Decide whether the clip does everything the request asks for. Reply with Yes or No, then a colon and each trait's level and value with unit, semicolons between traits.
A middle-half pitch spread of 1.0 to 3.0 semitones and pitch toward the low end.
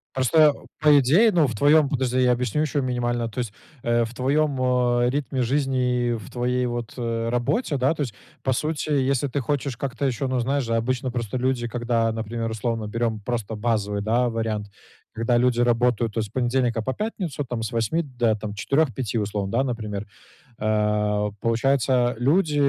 Yes: average, 2.7 semitones; low, 120 Hz